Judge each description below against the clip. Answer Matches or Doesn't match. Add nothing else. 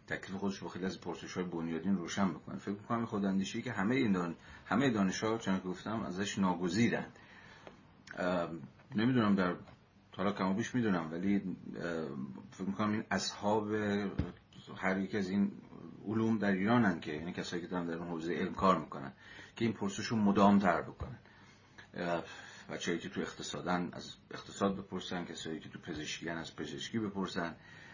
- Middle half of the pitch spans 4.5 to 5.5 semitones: Doesn't match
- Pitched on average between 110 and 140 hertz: Doesn't match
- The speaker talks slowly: Doesn't match